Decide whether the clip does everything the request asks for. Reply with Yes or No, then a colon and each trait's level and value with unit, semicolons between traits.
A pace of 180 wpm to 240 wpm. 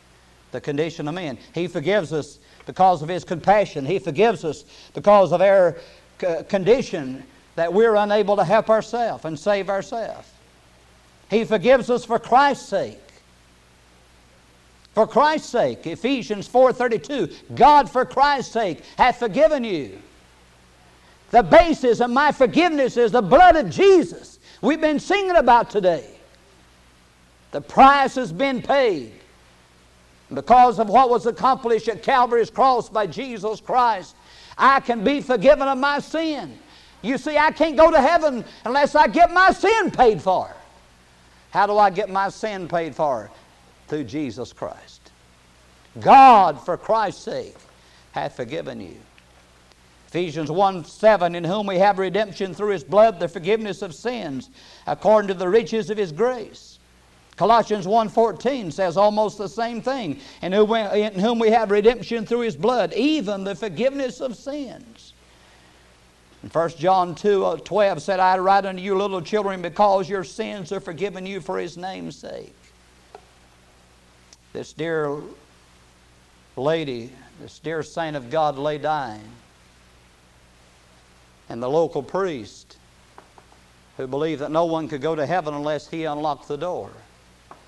No: average, 140 wpm